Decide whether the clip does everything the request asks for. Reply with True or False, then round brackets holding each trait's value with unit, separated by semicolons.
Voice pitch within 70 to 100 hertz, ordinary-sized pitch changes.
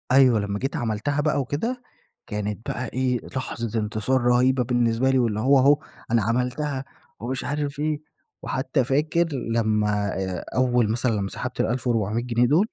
False (125 Hz; 3.3 semitones)